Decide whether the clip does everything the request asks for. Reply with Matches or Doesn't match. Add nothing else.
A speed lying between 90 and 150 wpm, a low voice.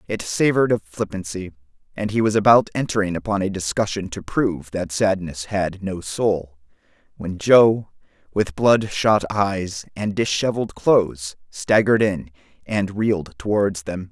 Matches